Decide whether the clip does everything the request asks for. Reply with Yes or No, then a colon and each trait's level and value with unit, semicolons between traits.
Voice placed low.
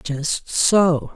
No: medium, 155 Hz